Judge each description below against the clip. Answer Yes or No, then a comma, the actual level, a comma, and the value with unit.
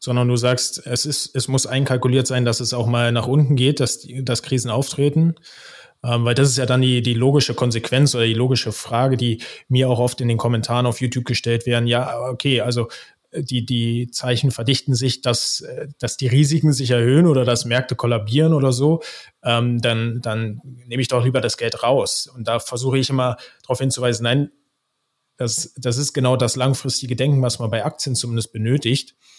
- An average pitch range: No, narrow, 1.9 semitones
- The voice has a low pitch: Yes, low, 125 Hz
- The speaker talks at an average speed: No, fast, 200 wpm